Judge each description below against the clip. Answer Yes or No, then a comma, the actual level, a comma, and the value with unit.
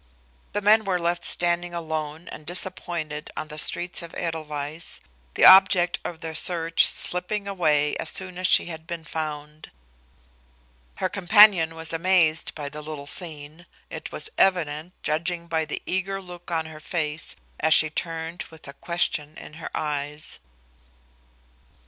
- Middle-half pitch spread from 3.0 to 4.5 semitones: No, narrow, 2.5 semitones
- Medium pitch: Yes, medium, 165 Hz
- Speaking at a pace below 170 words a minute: Yes, average, 150 wpm